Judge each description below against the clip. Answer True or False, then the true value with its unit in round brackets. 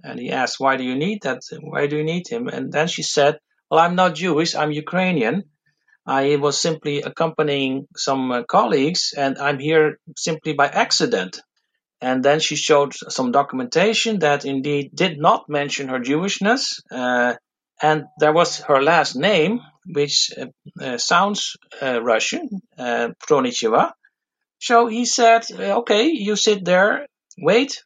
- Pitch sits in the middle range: True (155 Hz)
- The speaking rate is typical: True (155 wpm)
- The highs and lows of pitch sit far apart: True (5.8 semitones)